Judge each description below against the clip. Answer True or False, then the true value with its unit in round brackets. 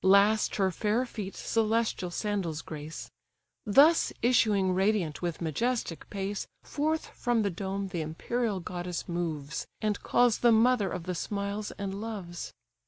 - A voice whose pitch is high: True (200 Hz)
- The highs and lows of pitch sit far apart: False (4.0 semitones)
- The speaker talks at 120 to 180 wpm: True (140 wpm)